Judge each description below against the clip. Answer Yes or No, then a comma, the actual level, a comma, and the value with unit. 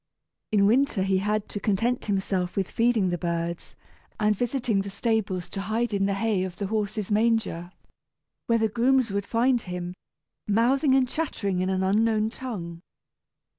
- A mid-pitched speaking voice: No, high, 210 Hz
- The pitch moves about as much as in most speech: Yes, average, 3.4 semitones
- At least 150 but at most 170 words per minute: Yes, average, 165 wpm